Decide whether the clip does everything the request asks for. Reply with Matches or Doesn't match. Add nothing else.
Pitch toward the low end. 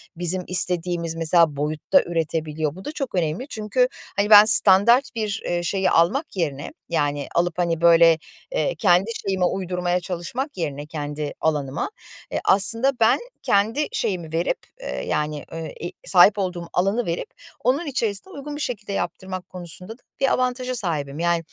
Doesn't match